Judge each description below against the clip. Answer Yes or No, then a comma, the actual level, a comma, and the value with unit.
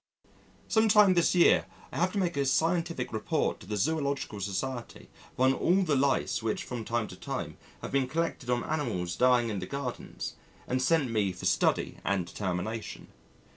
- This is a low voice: Yes, low, 130 Hz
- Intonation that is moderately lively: No, wide, 6.8 semitones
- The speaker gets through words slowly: No, average, 175 wpm